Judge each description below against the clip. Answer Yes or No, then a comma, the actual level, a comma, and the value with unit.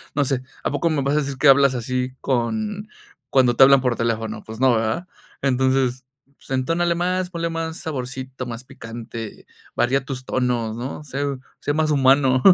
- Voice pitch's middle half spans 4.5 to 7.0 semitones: No, average, 2.9 semitones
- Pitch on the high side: No, low, 130 Hz